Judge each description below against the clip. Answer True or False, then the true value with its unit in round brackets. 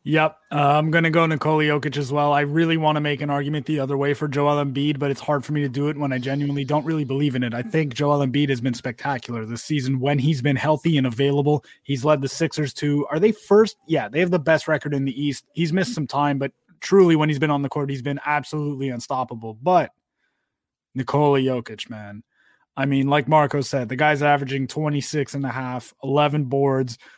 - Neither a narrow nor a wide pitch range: False (1.8 semitones)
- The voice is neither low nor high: True (145 Hz)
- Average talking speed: False (230 wpm)